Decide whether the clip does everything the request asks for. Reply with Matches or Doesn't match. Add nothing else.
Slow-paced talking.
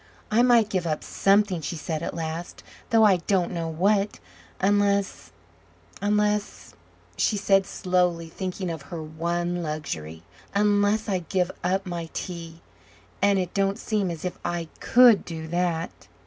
Doesn't match